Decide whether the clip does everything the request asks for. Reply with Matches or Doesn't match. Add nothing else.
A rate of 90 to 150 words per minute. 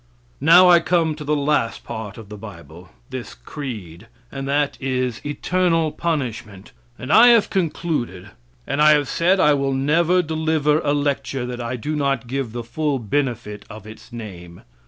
Doesn't match